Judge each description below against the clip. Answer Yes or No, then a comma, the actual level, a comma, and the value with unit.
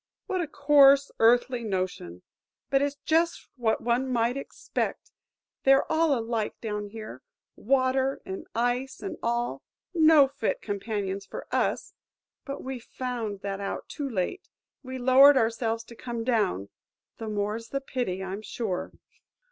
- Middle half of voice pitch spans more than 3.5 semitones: Yes, average, 4.3 semitones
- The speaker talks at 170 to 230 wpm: No, average, 145 wpm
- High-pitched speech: Yes, high, 240 Hz